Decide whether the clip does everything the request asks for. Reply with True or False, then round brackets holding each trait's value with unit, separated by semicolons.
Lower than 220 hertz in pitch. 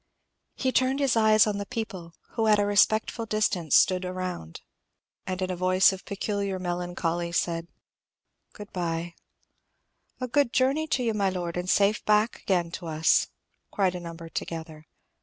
True (185 Hz)